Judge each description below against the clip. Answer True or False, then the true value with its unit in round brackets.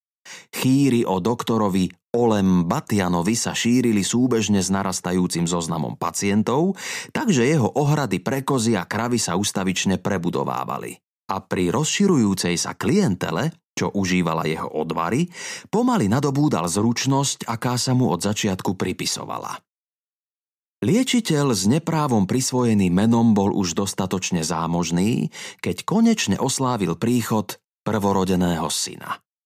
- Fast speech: False (110 wpm)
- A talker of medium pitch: False (105 Hz)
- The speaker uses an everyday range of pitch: False (6.0 semitones)